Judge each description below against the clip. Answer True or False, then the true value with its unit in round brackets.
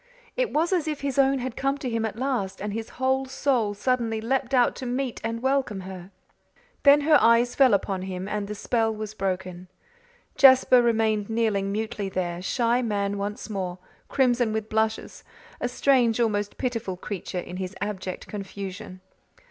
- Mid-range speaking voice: False (220 Hz)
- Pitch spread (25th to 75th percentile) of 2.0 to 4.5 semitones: True (4.2 semitones)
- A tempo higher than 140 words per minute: True (170 wpm)